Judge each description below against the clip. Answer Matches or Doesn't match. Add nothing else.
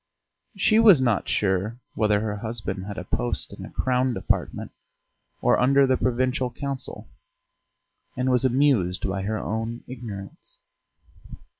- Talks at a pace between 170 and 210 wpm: Doesn't match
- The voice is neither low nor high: Doesn't match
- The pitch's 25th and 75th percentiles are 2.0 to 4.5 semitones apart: Matches